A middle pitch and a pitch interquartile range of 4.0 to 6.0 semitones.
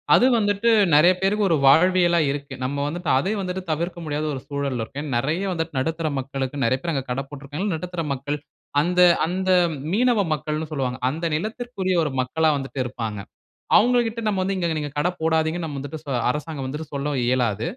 Yes: medium, 155 Hz; average, 4.6 semitones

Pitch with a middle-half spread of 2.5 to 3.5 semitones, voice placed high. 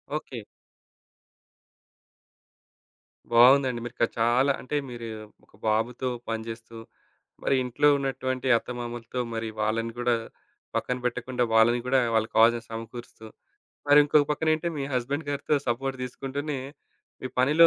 No: average, 2.8 semitones; low, 125 Hz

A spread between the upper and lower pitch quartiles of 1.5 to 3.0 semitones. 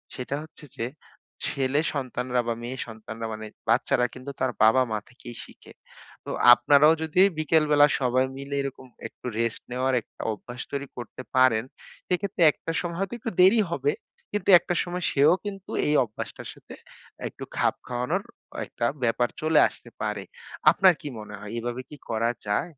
No: average, 4.5 semitones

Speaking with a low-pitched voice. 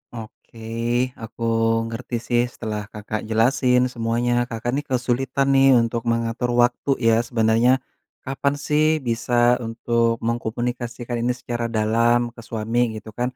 Yes: low, 120 Hz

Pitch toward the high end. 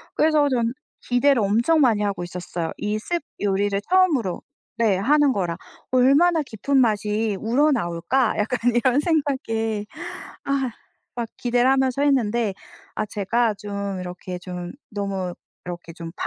Yes: high, 225 Hz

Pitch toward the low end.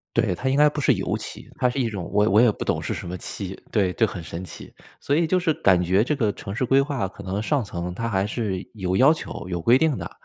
Yes: low, 110 Hz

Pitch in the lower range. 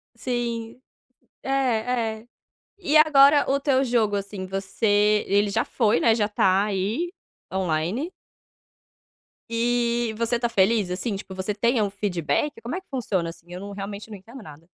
No: high, 220 Hz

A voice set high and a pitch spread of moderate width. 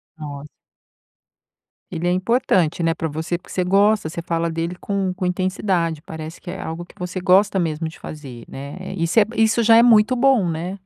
No: medium, 175 Hz; average, 3.4 semitones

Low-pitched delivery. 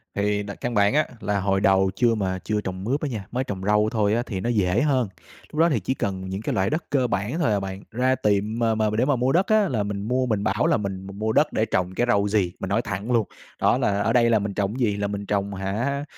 Yes: low, 105 Hz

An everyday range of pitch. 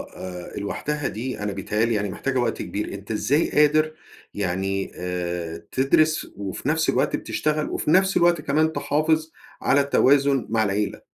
No: wide, 7.2 semitones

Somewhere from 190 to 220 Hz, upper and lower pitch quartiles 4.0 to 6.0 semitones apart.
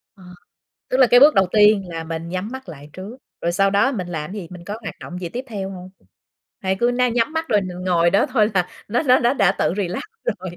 Yes: high, 195 Hz; average, 4.9 semitones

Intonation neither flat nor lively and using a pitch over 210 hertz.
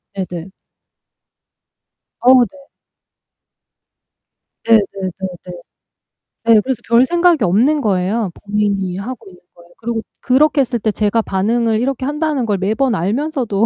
Yes: average, 4.8 semitones; high, 225 Hz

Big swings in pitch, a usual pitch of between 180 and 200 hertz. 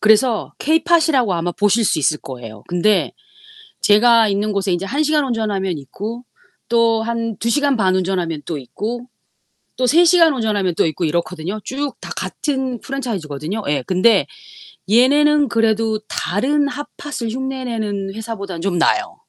No: wide, 5.7 semitones; high, 220 Hz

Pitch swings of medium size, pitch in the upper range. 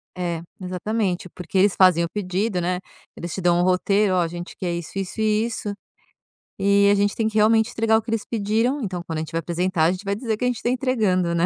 Yes: average, 3.6 semitones; high, 195 Hz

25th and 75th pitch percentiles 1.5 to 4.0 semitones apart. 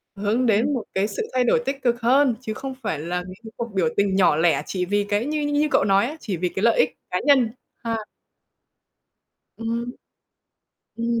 No: average, 4.4 semitones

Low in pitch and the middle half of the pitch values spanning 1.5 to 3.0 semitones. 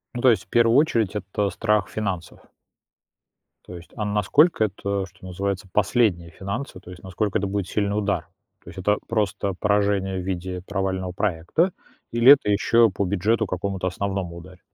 Yes: low, 100 Hz; narrow, 2.4 semitones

